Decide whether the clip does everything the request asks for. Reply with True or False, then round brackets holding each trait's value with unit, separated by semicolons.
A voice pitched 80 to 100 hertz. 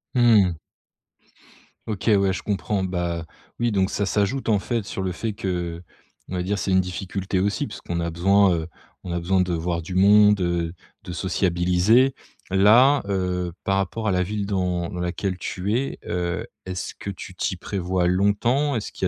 True (95 Hz)